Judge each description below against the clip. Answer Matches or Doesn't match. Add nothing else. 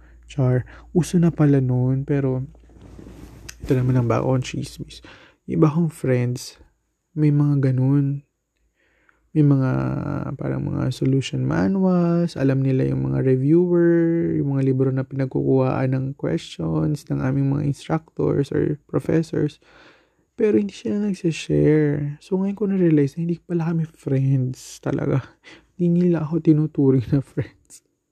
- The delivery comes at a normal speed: Matches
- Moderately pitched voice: Matches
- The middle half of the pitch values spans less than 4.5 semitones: Matches